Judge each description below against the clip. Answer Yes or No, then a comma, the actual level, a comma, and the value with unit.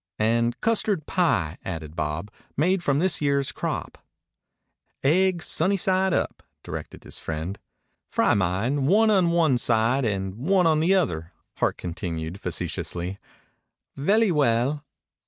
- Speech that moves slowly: Yes, slow, 130 wpm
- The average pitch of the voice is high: No, low, 135 Hz